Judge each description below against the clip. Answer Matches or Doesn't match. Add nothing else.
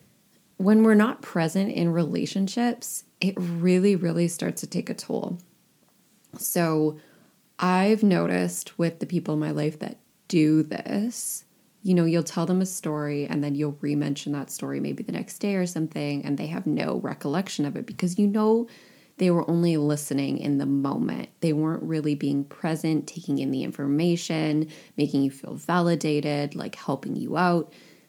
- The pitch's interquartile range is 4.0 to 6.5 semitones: Matches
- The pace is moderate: Matches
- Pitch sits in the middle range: Matches